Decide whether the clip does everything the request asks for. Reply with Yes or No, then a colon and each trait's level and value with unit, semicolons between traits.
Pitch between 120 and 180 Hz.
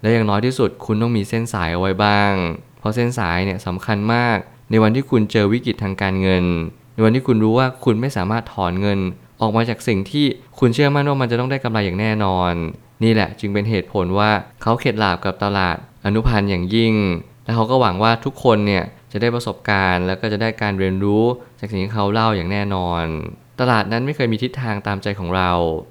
No: low, 110 Hz